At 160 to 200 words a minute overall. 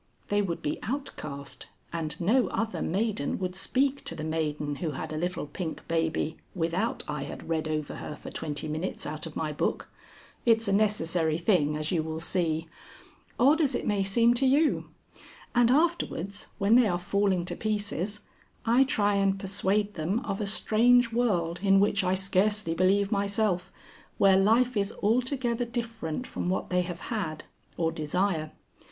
Yes: average, 170 wpm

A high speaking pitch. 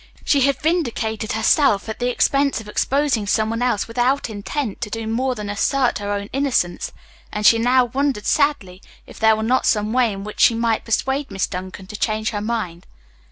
Yes: high, 225 Hz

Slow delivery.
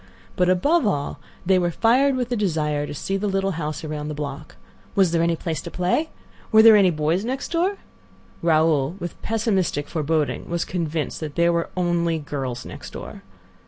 No: average, 185 wpm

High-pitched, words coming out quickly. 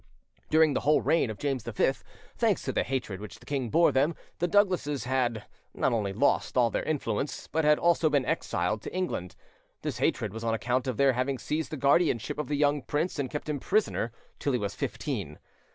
No: low, 135 Hz; fast, 210 wpm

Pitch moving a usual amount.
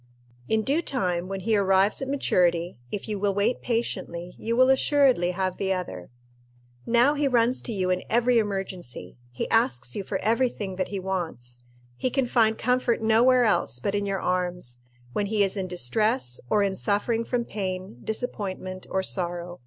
Yes: average, 4.3 semitones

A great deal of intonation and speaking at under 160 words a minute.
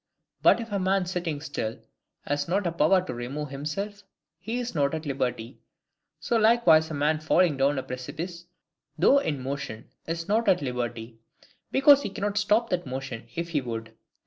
No: wide, 6.3 semitones; average, 175 wpm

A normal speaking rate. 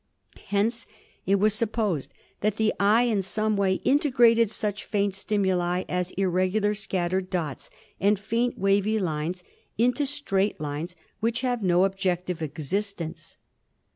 No: slow, 130 wpm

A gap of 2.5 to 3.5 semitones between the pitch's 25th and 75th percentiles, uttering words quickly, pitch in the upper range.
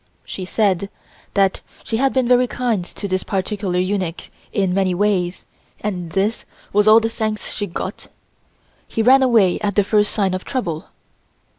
No: average, 3.0 semitones; average, 165 wpm; high, 205 Hz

